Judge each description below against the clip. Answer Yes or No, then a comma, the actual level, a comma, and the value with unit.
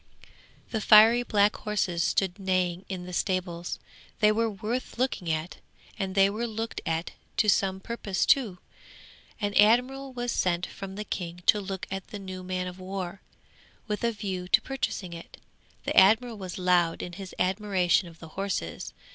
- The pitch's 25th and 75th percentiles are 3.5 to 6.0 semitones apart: No, average, 2.8 semitones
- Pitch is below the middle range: No, high, 195 Hz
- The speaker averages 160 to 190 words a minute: Yes, average, 170 wpm